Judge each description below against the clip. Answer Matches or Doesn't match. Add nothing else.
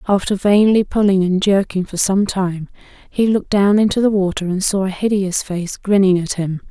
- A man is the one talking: Doesn't match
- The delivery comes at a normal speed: Matches